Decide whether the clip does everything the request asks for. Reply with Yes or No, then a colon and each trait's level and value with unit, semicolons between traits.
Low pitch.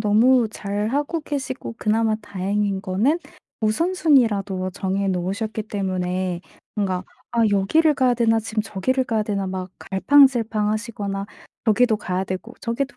No: high, 215 Hz